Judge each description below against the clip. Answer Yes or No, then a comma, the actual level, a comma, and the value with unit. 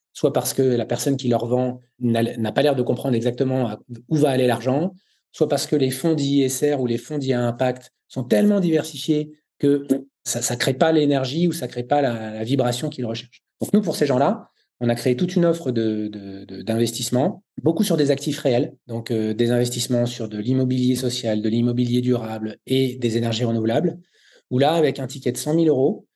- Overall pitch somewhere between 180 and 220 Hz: No, low, 125 Hz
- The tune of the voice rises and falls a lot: No, average, 3.4 semitones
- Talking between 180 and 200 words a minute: No, average, 215 wpm